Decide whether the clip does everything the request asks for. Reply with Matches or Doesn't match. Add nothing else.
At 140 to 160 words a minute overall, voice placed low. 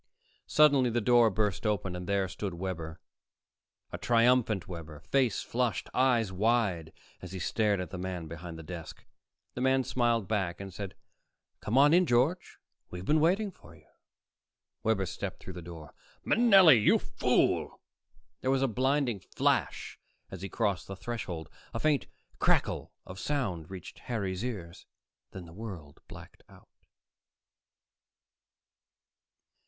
Matches